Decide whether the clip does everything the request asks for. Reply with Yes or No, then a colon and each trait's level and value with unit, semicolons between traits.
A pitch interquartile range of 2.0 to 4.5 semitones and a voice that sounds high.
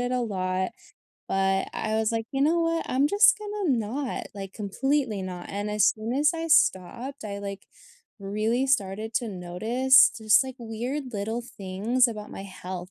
No: average, 5.0 semitones; high, 220 Hz